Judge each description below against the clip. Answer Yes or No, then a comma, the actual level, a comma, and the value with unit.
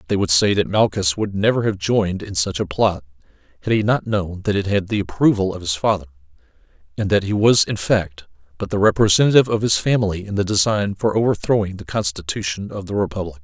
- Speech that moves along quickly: Yes, fast, 210 wpm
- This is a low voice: Yes, very low, 95 Hz